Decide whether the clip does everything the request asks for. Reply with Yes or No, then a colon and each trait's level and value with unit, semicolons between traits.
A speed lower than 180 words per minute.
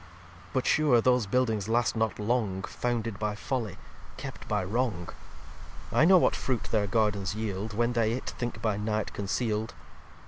Yes: average, 165 wpm